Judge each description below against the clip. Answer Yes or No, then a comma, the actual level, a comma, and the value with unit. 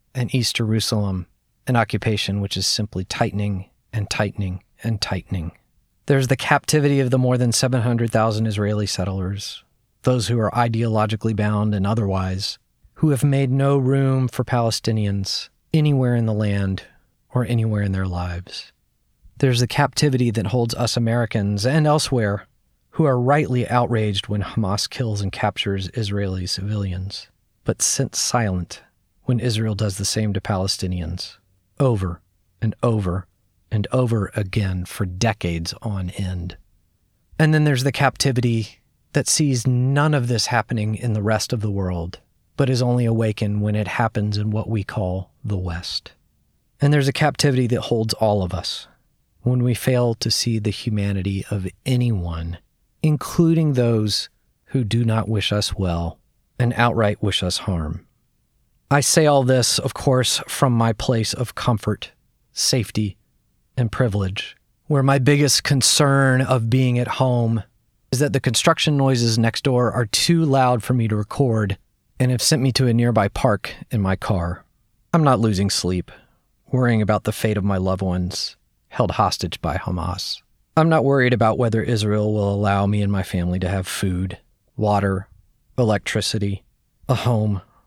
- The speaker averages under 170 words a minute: Yes, average, 155 wpm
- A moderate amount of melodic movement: Yes, average, 4.1 semitones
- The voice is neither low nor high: No, low, 110 Hz